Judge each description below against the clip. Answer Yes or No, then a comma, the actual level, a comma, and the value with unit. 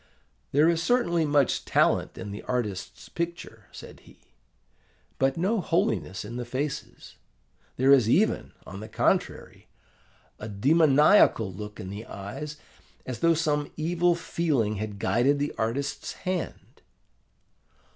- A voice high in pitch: No, medium, 140 Hz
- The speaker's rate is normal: No, slow, 130 wpm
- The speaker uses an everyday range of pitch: No, wide, 7.3 semitones